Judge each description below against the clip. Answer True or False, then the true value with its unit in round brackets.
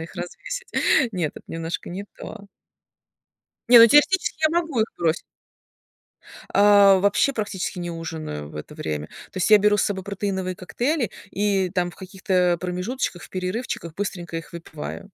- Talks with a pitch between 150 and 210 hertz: True (190 Hz)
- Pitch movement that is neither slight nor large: True (3.2 semitones)